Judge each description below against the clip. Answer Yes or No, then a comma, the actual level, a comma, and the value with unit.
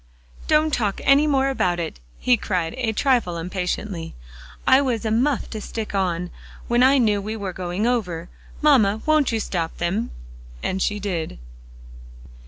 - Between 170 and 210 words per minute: No, average, 160 wpm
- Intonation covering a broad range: Yes, wide, 5.9 semitones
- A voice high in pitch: Yes, high, 215 Hz